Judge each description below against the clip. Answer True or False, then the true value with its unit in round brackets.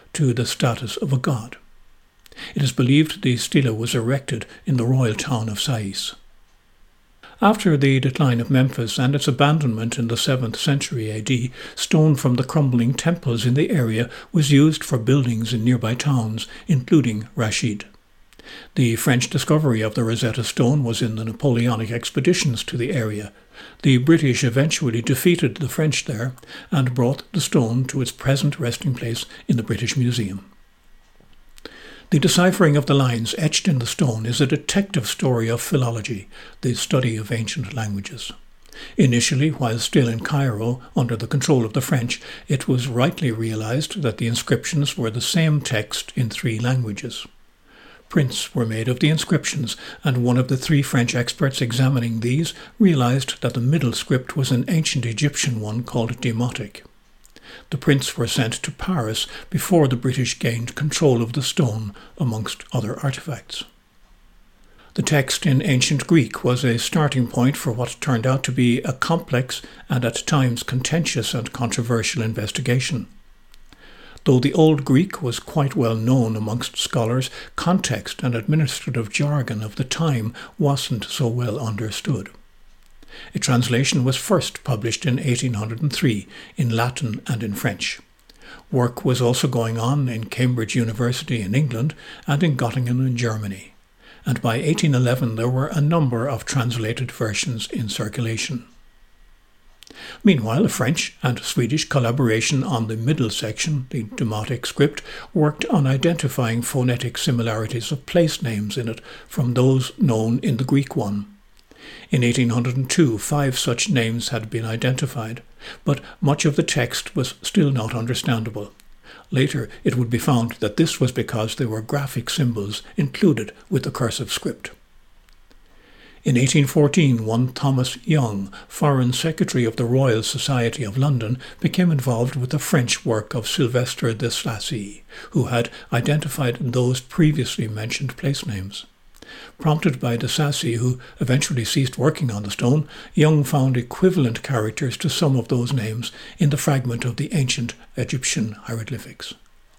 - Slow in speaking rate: False (155 wpm)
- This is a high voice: False (125 Hz)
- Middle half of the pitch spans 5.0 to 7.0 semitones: False (3.7 semitones)